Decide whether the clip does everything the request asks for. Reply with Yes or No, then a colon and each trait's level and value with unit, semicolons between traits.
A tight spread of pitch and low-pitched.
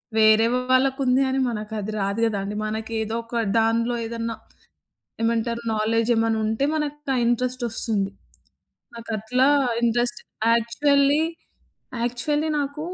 No: narrow, 2.3 semitones; high, 230 Hz